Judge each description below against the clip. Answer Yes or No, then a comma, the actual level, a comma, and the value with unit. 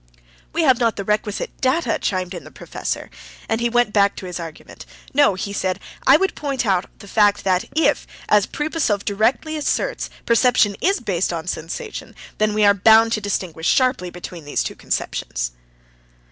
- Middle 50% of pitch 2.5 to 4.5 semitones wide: No, average, 5.2 semitones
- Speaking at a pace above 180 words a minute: No, average, 175 wpm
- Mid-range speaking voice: No, high, 210 Hz